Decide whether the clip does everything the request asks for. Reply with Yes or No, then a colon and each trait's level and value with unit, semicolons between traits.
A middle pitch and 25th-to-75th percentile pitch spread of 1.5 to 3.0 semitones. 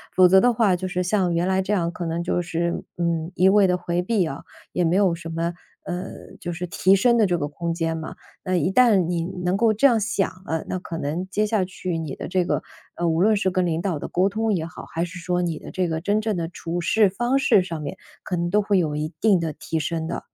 Yes: medium, 180 Hz; average, 2.7 semitones